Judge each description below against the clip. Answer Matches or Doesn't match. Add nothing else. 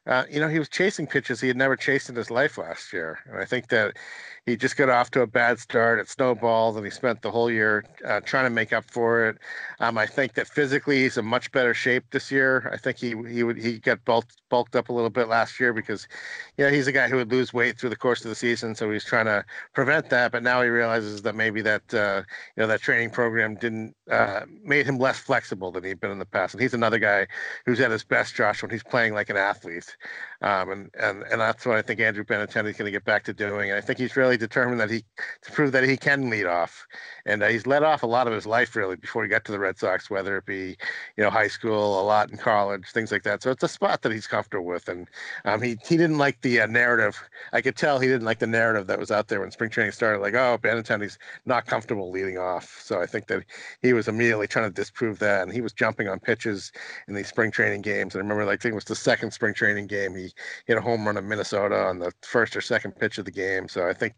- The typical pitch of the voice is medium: Doesn't match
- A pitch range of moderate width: Matches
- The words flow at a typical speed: Doesn't match